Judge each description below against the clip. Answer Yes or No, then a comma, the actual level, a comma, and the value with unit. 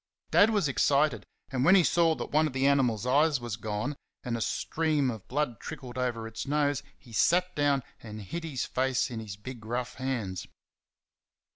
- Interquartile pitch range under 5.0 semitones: Yes, average, 4.3 semitones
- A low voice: Yes, low, 130 Hz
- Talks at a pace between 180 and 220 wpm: Yes, average, 185 wpm